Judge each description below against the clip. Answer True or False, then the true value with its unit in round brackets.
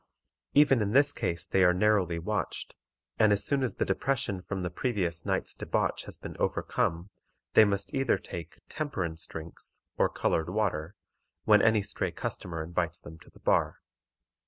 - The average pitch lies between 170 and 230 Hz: False (95 Hz)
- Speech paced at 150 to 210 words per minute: True (165 wpm)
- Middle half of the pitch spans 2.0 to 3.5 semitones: False (4.2 semitones)